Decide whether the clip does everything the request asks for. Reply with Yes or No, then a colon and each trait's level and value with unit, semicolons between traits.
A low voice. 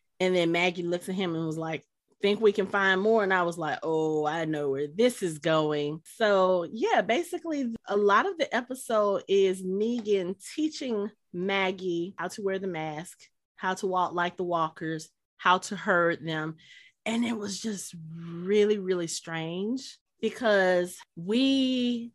No: medium, 185 Hz